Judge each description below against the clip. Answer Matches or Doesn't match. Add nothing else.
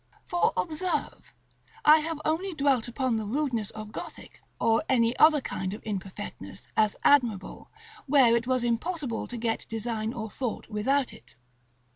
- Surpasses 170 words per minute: Doesn't match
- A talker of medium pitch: Doesn't match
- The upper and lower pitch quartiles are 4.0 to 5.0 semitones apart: Matches